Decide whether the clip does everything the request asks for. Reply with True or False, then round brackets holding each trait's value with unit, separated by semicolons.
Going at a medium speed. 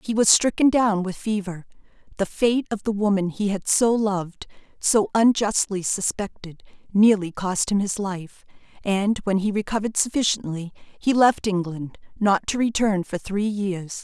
True (160 wpm)